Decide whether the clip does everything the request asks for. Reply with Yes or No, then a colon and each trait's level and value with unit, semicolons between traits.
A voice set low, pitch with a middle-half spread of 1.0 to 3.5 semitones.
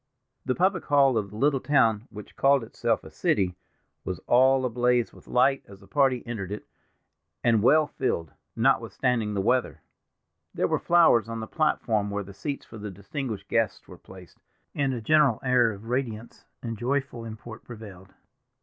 No: low, 120 Hz; average, 4.1 semitones